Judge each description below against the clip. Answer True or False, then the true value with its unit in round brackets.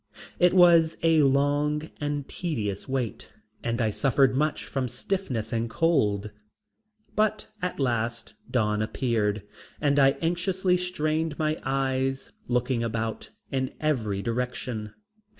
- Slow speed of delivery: True (120 wpm)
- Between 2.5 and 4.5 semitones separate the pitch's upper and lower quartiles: False (5.1 semitones)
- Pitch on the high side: False (135 Hz)